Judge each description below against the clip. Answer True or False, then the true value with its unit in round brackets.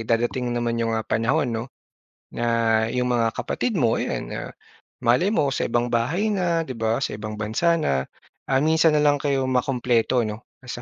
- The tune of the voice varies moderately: True (4.2 semitones)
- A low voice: True (120 Hz)